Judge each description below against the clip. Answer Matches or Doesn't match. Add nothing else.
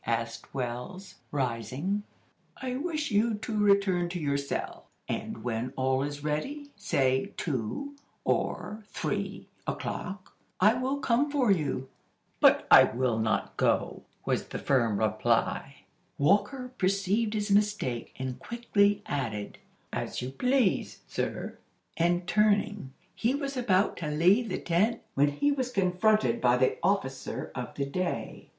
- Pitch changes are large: Matches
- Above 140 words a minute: Doesn't match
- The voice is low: Doesn't match